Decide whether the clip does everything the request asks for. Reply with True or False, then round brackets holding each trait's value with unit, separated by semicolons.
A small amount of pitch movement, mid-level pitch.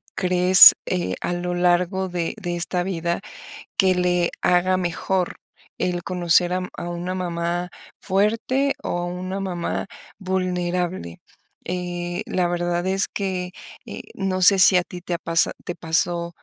True (1.1 semitones; 180 Hz)